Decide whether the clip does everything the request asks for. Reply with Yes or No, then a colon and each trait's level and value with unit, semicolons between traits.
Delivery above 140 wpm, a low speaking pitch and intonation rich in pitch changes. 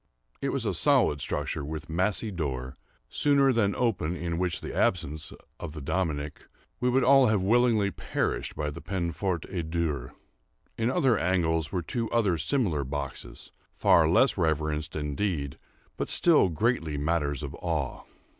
Yes: average, 155 wpm; very low, 85 Hz; wide, 6.0 semitones